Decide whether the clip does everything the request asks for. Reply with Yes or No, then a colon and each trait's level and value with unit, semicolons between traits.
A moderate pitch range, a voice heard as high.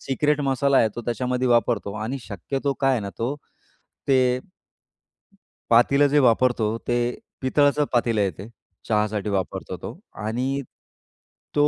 No: average, 3.8 semitones; low, 125 Hz